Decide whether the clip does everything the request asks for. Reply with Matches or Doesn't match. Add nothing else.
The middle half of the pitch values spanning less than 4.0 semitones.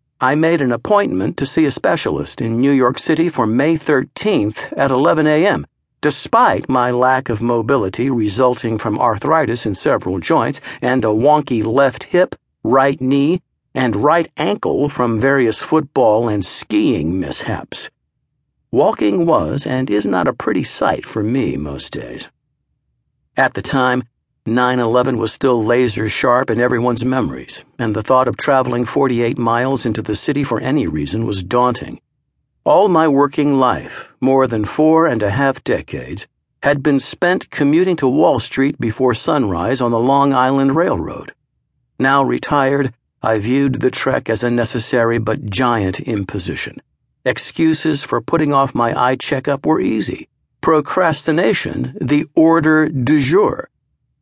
Matches